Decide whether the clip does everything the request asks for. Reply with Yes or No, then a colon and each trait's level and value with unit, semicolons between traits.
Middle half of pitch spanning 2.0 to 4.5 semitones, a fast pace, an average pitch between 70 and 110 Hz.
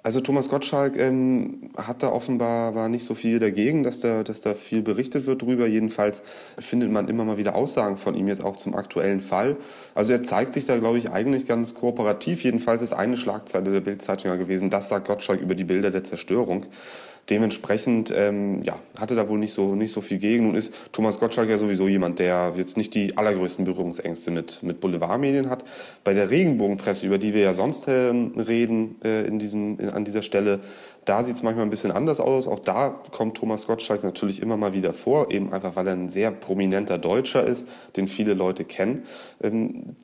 Yes: average, 2.9 semitones; fast, 205 wpm; low, 105 Hz